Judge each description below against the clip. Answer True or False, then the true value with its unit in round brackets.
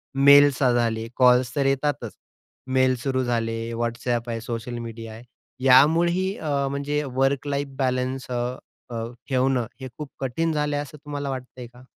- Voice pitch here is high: False (130 Hz)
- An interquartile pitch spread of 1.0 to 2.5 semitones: False (2.9 semitones)